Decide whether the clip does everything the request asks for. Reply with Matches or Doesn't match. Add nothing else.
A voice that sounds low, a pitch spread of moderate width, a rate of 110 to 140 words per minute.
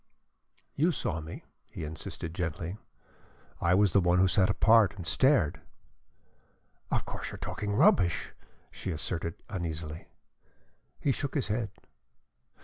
Matches